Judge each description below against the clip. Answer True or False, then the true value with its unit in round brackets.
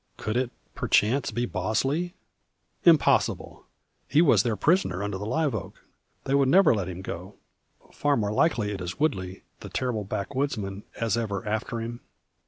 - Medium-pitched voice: False (115 Hz)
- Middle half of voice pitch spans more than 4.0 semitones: True (5.6 semitones)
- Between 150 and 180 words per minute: True (160 wpm)